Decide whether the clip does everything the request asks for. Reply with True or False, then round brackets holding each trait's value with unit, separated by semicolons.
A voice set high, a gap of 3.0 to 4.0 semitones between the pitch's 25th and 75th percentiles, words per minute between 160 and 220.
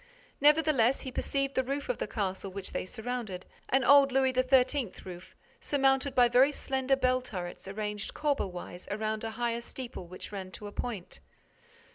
False (245 Hz; 4.8 semitones; 170 wpm)